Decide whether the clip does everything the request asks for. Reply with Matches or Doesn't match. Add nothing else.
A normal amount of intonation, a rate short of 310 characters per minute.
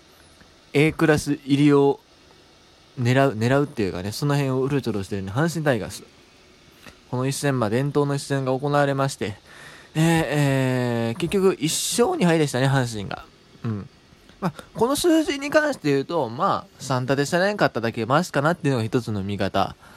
Doesn't match